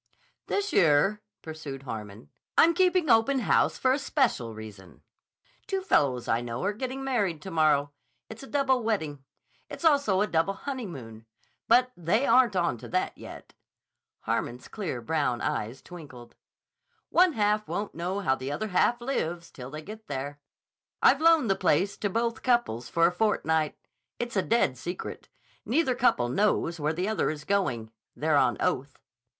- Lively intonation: Yes, wide, 9.0 semitones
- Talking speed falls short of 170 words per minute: Yes, average, 160 wpm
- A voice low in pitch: No, medium, 180 Hz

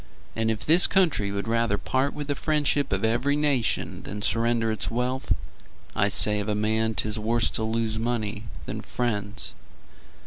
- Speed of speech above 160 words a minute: Yes, average, 170 wpm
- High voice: No, low, 115 Hz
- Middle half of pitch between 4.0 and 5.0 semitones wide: No, average, 3.3 semitones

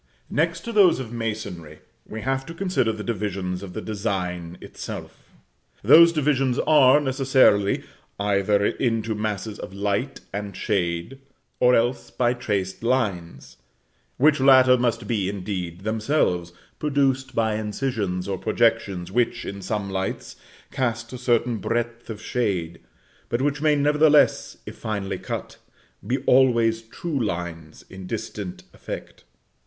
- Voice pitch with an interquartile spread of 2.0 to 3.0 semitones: No, average, 4.9 semitones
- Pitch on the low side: Yes, low, 110 Hz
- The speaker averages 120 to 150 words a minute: Yes, average, 140 wpm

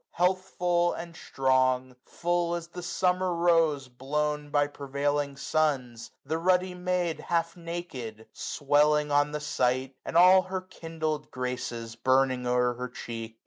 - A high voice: No, medium, 150 Hz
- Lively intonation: No, average, 5.0 semitones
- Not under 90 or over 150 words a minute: Yes, average, 140 wpm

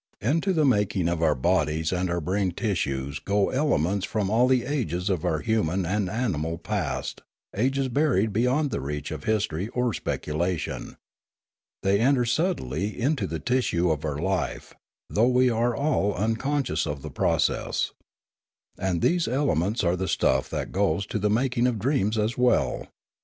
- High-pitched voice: No, low, 100 Hz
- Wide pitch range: Yes, wide, 6.4 semitones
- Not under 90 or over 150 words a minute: No, average, 165 wpm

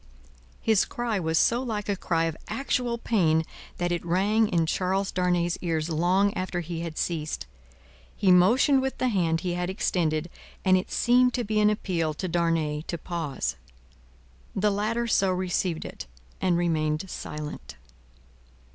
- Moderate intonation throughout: Yes, average, 4.1 semitones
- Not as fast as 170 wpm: Yes, average, 155 wpm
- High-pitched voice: No, medium, 180 Hz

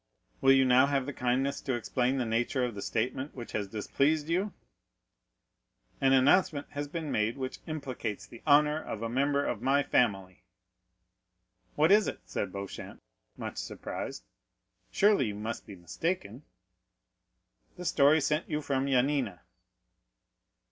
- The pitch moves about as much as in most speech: Yes, average, 4.0 semitones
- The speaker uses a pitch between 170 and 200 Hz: No, low, 135 Hz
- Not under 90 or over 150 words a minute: Yes, average, 145 wpm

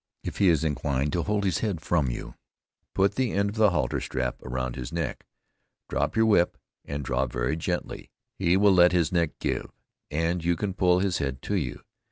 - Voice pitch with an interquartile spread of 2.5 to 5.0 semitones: No, wide, 5.5 semitones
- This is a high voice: No, very low, 85 Hz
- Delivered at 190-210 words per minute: Yes, fast, 205 wpm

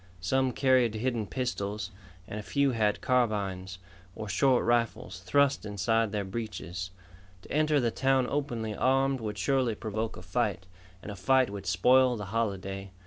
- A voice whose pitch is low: Yes, low, 110 Hz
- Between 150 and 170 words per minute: Yes, average, 155 wpm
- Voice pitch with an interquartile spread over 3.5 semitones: Yes, average, 4.4 semitones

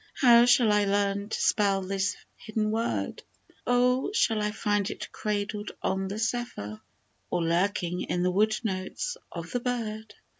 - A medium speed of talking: Yes, average, 155 wpm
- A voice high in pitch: Yes, high, 210 Hz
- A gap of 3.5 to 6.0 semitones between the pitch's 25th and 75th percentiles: No, average, 2.7 semitones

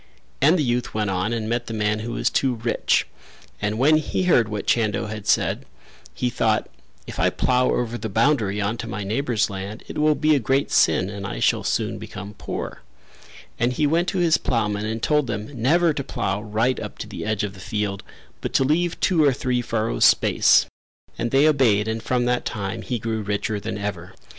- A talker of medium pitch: No, low, 115 Hz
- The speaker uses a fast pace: Yes, fast, 210 wpm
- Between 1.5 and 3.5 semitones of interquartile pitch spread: No, average, 4.2 semitones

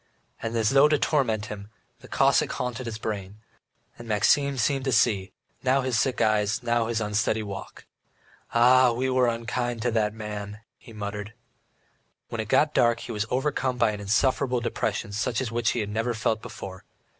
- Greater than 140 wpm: Yes, average, 180 wpm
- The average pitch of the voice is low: Yes, low, 115 Hz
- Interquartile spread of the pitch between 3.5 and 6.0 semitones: No, average, 2.9 semitones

